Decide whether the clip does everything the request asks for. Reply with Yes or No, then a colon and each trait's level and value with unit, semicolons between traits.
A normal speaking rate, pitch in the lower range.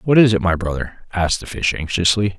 No: fast, 225 wpm; very low, 95 Hz